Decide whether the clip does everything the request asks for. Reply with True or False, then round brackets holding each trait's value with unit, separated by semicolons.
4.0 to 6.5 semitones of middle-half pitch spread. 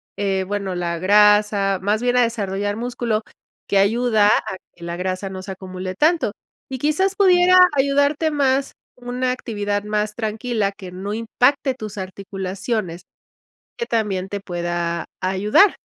True (4.5 semitones)